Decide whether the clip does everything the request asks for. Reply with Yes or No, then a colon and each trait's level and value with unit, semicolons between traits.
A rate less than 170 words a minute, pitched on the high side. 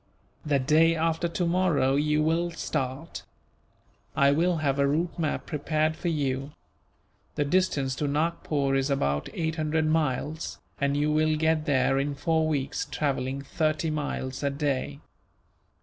No: average, 145 wpm; medium, 150 Hz